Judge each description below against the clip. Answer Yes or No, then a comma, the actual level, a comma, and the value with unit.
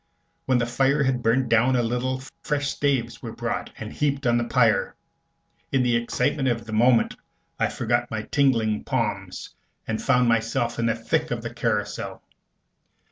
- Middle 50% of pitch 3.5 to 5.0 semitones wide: No, narrow, 2.4 semitones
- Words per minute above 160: Yes, average, 170 wpm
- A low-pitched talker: Yes, low, 120 Hz